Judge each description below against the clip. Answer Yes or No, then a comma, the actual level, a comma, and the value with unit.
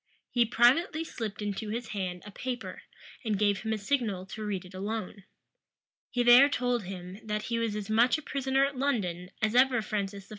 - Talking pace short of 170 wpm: No, average, 195 wpm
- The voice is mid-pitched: No, high, 220 Hz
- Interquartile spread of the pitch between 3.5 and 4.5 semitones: Yes, average, 3.8 semitones